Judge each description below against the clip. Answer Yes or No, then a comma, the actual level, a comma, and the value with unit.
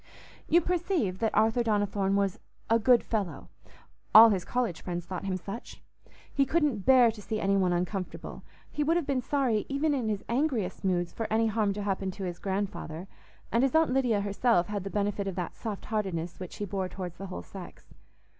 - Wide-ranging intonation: No, average, 4.2 semitones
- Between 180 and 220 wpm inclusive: Yes, average, 195 wpm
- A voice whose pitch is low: No, high, 205 Hz